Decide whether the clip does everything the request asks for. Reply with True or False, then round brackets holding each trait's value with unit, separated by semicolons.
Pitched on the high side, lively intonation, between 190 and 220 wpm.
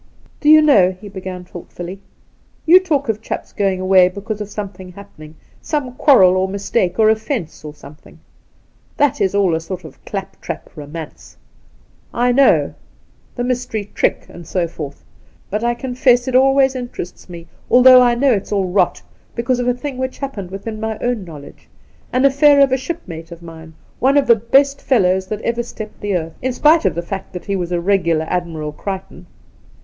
True (205 Hz; 5.8 semitones; 195 wpm)